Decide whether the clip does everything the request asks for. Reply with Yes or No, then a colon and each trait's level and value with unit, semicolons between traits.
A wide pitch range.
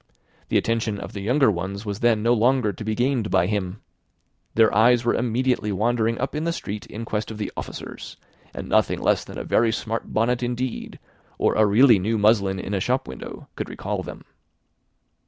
No: average, 2.7 semitones